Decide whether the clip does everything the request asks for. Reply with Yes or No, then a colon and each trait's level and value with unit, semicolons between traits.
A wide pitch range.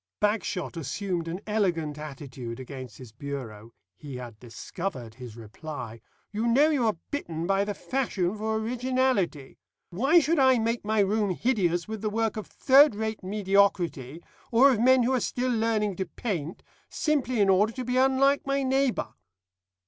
Yes: wide, 7.7 semitones